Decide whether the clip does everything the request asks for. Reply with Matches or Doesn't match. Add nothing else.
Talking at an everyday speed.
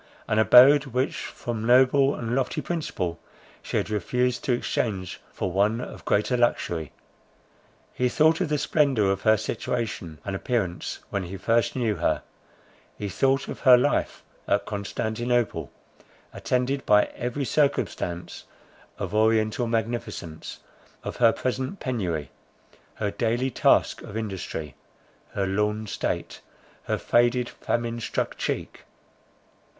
Doesn't match